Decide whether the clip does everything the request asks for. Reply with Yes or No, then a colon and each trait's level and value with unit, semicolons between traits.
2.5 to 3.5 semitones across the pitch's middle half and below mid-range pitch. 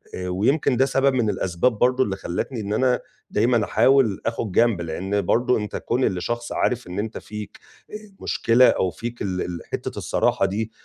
No: average, 4.4 semitones; low, 110 Hz